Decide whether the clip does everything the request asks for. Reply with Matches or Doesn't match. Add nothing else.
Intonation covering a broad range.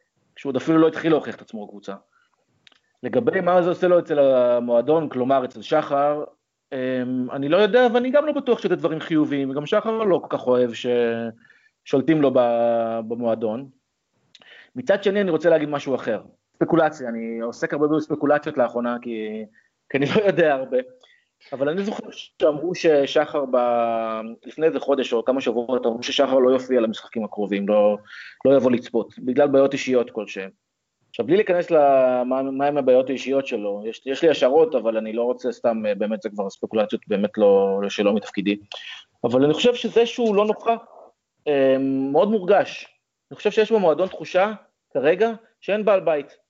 Matches